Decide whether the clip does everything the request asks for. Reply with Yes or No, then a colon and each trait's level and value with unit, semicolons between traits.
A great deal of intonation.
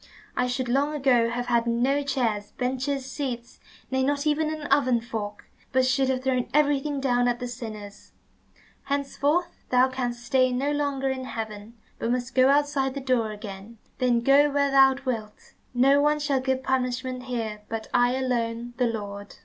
No: narrow, 2.5 semitones